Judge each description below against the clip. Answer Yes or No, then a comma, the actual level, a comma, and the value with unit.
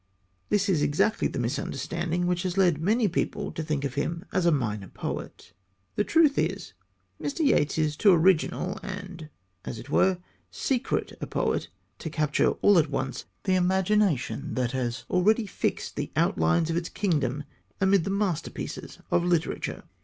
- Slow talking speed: No, average, 160 wpm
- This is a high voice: No, medium, 170 Hz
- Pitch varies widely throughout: No, average, 4.8 semitones